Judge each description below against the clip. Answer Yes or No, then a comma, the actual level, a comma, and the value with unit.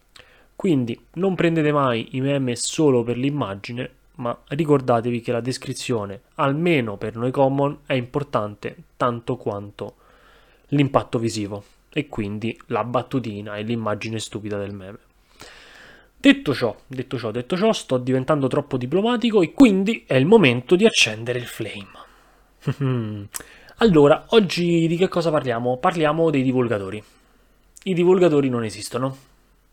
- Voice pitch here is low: Yes, low, 130 Hz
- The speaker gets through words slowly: No, average, 130 wpm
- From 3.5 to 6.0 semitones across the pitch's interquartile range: Yes, average, 4.8 semitones